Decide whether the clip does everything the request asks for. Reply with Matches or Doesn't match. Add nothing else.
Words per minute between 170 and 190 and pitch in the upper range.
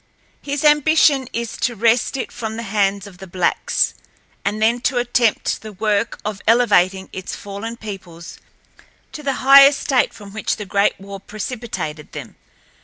Doesn't match